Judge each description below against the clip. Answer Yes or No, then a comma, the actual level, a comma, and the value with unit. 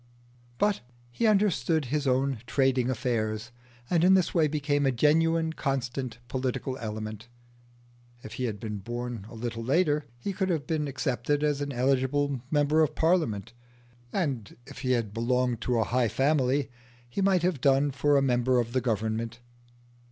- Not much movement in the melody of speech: No, average, 4.0 semitones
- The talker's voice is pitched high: No, low, 130 Hz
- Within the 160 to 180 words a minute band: Yes, average, 165 wpm